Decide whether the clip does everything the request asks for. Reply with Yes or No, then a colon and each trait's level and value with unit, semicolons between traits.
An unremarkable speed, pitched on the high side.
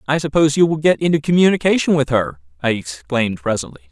No: average, 185 wpm; medium, 140 Hz